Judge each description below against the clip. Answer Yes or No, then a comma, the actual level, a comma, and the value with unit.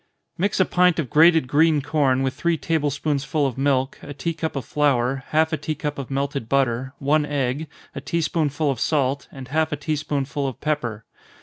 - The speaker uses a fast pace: Yes, fast, 210 wpm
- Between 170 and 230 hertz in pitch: No, medium, 145 Hz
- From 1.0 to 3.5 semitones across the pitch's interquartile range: Yes, narrow, 2.6 semitones